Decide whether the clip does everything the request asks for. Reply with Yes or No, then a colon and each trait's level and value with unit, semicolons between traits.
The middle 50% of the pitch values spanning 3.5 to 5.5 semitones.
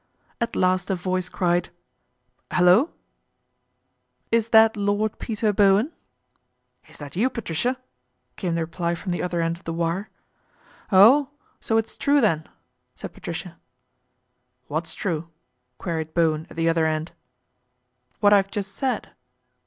Yes: average, 4.6 semitones